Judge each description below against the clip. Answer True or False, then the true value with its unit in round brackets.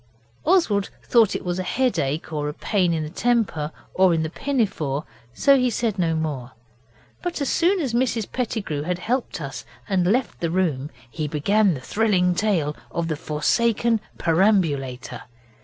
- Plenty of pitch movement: True (6.9 semitones)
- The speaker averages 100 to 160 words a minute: True (155 wpm)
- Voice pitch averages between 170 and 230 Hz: True (185 Hz)